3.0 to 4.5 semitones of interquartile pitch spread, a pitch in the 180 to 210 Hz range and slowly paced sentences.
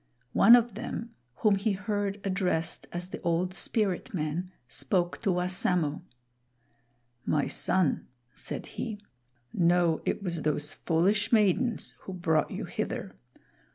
Yes: average, 3.3 semitones; medium, 185 Hz; slow, 125 wpm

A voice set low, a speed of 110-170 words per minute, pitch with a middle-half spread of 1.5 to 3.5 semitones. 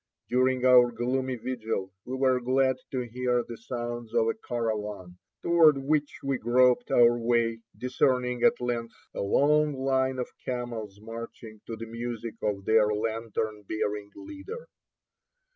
Yes: low, 120 Hz; average, 145 wpm; narrow, 2.4 semitones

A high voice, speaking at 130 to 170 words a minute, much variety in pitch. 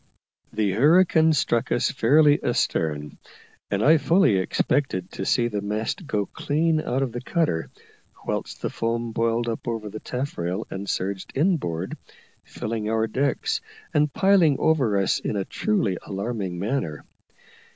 No: low, 115 Hz; average, 145 wpm; wide, 6.6 semitones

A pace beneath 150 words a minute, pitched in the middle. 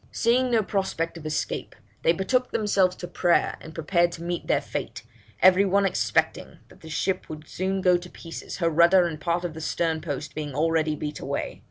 No: average, 200 wpm; medium, 170 Hz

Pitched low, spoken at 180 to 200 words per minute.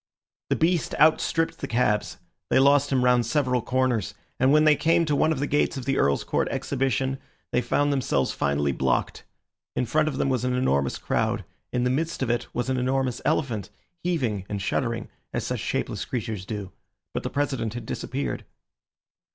Yes: low, 130 Hz; average, 185 wpm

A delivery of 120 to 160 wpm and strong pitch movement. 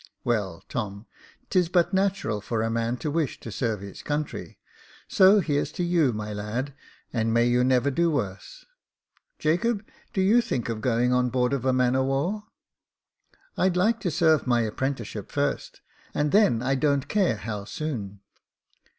No: average, 175 wpm; wide, 6.8 semitones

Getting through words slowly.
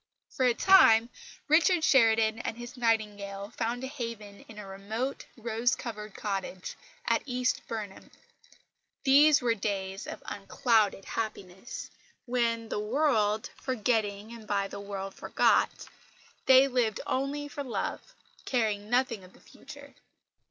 Yes: slow, 130 wpm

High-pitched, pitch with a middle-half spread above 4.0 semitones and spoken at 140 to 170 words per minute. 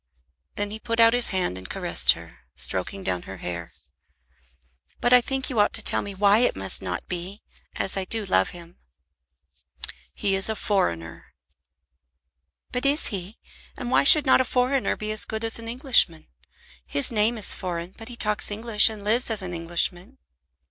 No: high, 205 Hz; average, 4.8 semitones; average, 185 wpm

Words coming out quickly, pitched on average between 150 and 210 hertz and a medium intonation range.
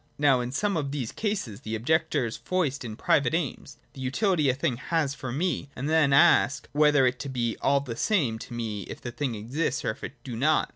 No: fast, 220 wpm; low, 135 Hz; average, 4.1 semitones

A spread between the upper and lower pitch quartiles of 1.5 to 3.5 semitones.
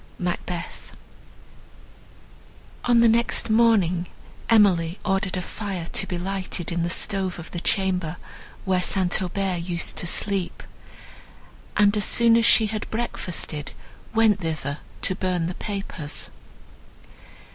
Yes: average, 3.2 semitones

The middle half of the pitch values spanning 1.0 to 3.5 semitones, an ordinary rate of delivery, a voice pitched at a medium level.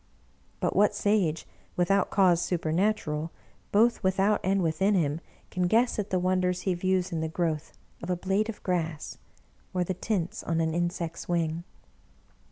Yes: average, 2.8 semitones; average, 160 wpm; medium, 180 Hz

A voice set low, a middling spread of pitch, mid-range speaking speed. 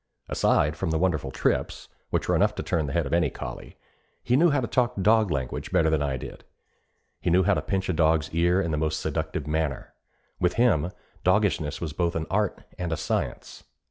No: very low, 85 Hz; average, 3.5 semitones; fast, 210 wpm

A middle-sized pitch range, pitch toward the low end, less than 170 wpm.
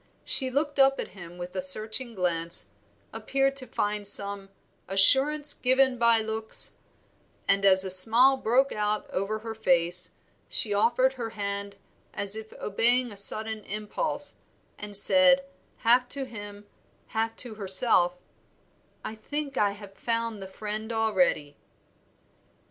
No: average, 3.8 semitones; high, 220 Hz; slow, 135 wpm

